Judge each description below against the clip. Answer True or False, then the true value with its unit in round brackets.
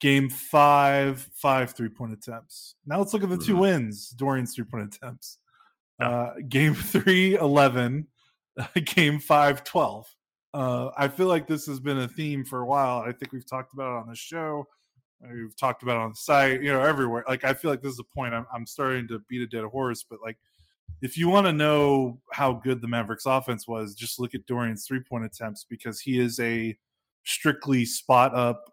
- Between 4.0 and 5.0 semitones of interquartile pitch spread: False (3.2 semitones)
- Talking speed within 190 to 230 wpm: True (205 wpm)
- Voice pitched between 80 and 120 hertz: False (130 Hz)